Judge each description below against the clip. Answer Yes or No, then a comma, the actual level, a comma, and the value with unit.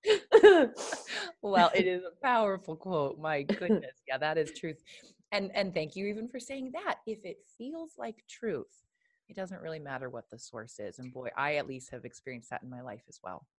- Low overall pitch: No, high, 190 Hz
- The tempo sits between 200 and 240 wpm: Yes, fast, 205 wpm